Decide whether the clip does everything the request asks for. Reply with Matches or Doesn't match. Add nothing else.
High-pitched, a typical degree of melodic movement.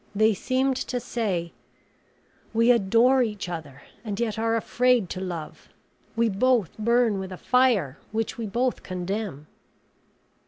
Matches